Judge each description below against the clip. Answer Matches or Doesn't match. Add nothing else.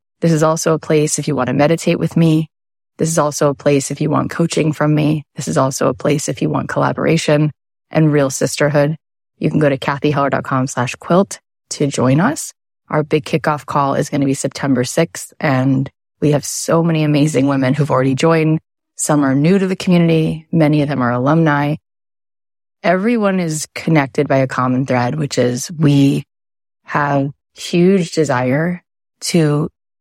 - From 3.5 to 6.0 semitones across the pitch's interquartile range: Doesn't match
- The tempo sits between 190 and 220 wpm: Doesn't match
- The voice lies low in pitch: Doesn't match